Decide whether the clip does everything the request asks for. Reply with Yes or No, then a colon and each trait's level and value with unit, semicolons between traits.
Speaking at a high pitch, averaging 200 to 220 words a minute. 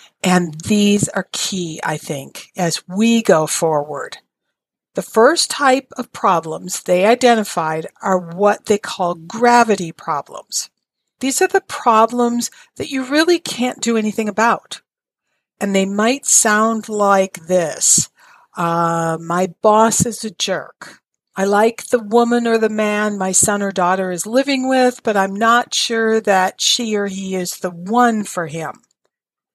No: high, 210 Hz; average, 150 wpm